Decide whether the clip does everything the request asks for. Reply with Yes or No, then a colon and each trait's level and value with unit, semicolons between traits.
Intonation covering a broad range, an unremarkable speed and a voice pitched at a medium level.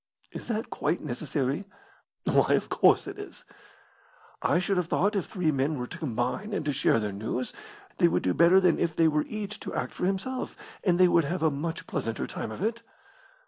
No: wide, 6.2 semitones; fast, 210 wpm; medium, 165 Hz